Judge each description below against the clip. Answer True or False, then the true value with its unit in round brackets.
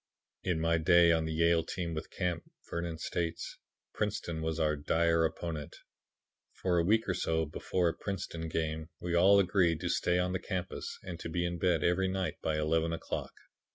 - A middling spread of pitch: False (1.7 semitones)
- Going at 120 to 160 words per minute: False (190 wpm)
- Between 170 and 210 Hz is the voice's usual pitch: False (85 Hz)